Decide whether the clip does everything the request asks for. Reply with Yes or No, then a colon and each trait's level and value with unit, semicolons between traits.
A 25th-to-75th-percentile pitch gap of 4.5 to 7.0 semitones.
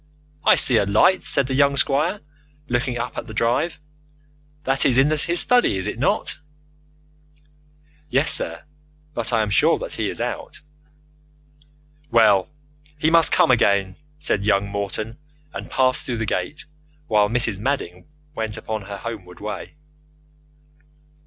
Yes: average, 5.1 semitones